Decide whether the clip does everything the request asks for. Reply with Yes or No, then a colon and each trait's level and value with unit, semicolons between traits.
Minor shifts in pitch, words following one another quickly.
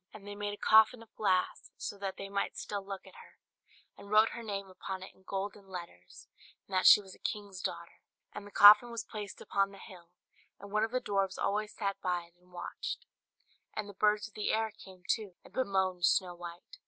Yes: narrow, 2.0 semitones; fast, 220 wpm